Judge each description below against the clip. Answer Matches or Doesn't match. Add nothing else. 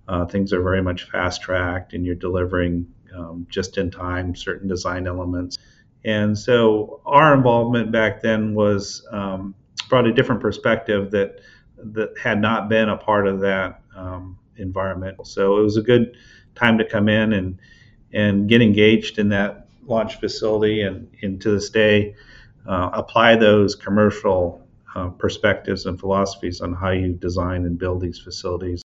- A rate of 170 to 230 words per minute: Doesn't match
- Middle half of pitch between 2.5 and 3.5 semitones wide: Matches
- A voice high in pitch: Doesn't match